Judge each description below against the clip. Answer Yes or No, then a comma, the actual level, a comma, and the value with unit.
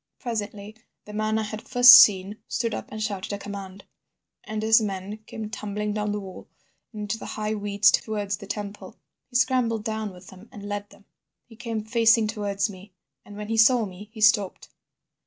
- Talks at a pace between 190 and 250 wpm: Yes, average, 195 wpm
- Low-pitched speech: No, high, 210 Hz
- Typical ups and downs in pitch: No, narrow, 1.5 semitones